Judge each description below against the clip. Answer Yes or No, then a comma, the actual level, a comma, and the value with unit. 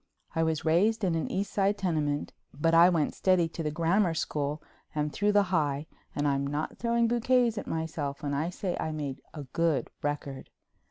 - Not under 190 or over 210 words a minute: Yes, average, 195 wpm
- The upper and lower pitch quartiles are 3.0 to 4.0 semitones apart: No, average, 4.5 semitones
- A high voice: No, medium, 160 Hz